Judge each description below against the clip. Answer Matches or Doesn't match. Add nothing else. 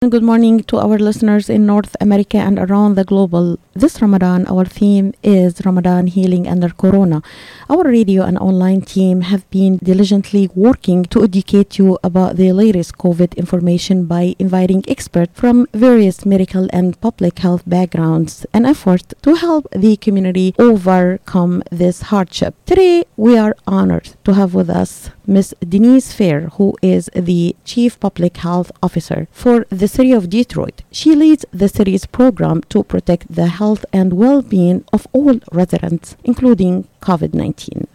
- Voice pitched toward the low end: Doesn't match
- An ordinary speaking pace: Doesn't match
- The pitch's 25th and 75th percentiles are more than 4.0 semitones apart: Doesn't match